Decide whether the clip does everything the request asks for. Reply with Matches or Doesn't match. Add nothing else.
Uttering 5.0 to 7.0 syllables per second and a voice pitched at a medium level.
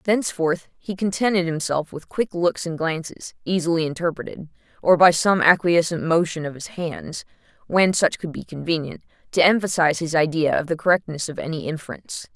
Matches